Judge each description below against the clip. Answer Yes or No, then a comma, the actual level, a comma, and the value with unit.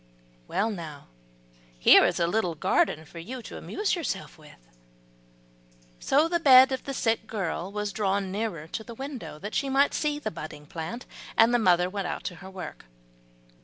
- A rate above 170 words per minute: Yes, average, 180 wpm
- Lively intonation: Yes, wide, 6.9 semitones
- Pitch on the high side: Yes, high, 205 Hz